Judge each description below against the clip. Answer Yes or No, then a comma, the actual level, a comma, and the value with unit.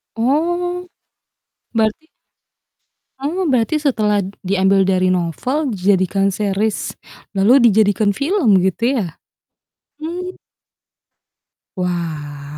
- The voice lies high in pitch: Yes, high, 210 Hz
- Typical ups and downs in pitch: No, wide, 6.9 semitones